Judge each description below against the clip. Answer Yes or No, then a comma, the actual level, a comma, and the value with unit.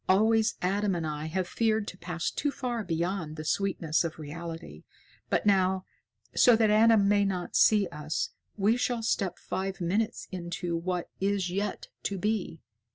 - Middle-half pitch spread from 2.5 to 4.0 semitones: Yes, average, 3.6 semitones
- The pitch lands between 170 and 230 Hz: Yes, high, 190 Hz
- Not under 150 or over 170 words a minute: Yes, average, 160 wpm